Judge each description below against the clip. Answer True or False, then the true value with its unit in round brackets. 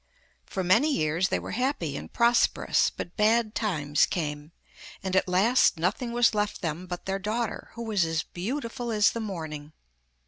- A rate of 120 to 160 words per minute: False (170 wpm)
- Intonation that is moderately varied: False (5.9 semitones)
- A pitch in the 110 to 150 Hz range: False (195 Hz)